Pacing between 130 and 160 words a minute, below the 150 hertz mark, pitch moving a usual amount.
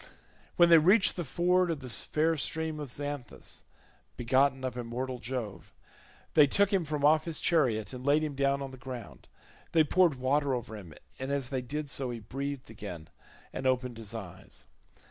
No: average, 185 wpm; low, 135 Hz; average, 3.9 semitones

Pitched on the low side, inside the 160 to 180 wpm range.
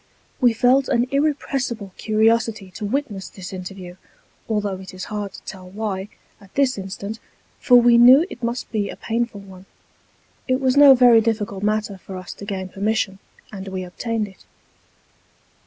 No: high, 215 Hz; average, 165 wpm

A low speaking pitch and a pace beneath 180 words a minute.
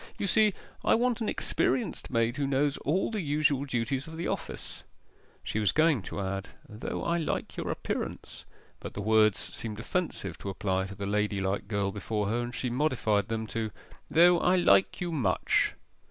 No: low, 120 Hz; average, 185 wpm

